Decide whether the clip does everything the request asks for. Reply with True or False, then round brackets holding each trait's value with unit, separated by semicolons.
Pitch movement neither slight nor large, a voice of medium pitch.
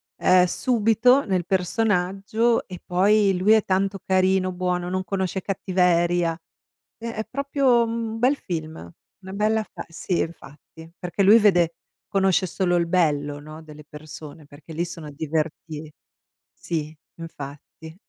True (3.9 semitones; 180 Hz)